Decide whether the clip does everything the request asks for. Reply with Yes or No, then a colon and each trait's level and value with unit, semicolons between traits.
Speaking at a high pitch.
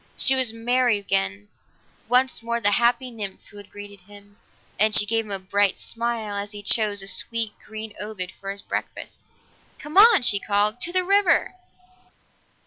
Yes: high, 215 Hz